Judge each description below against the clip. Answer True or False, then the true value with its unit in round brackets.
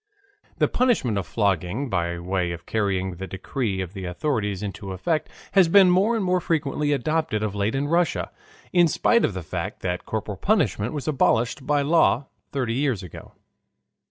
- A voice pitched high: False (115 Hz)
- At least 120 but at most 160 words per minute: False (175 wpm)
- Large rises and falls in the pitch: True (8.2 semitones)